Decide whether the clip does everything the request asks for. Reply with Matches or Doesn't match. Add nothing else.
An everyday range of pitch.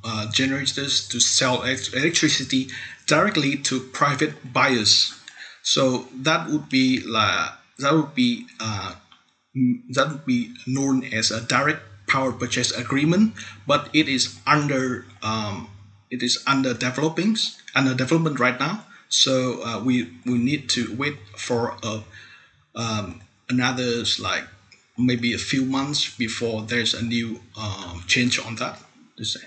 Matches